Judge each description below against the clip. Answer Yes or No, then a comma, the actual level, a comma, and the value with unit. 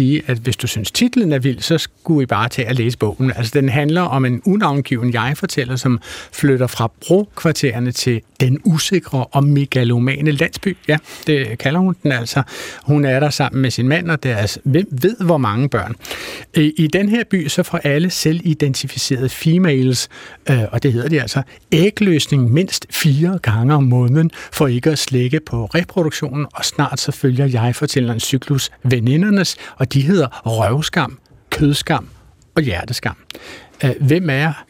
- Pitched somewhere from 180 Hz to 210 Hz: No, medium, 140 Hz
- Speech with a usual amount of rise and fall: Yes, average, 4.1 semitones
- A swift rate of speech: No, average, 170 wpm